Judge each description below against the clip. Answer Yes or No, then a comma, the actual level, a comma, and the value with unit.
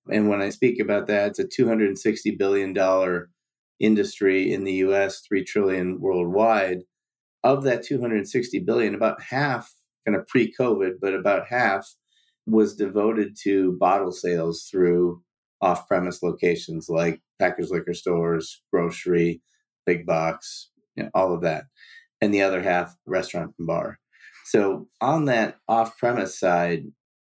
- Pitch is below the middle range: Yes, very low, 95 Hz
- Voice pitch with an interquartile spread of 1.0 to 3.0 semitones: No, average, 3.5 semitones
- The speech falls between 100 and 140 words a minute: Yes, slow, 135 wpm